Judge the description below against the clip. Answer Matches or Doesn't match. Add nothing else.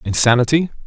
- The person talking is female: Doesn't match